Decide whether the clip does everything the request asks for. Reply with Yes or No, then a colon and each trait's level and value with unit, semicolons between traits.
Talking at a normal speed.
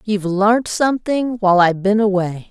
Yes: average, 165 wpm